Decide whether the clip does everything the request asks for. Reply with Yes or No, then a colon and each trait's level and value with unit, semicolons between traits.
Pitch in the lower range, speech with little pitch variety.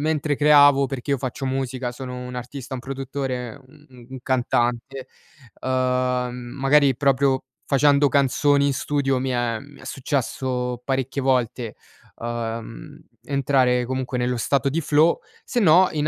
Yes: low, 130 Hz; narrow, 2.1 semitones